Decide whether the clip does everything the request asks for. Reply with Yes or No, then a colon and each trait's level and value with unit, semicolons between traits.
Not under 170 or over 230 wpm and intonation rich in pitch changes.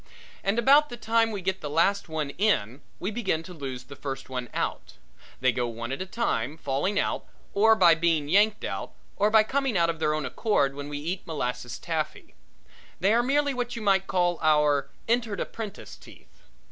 Yes: average, 200 wpm; wide, 7.1 semitones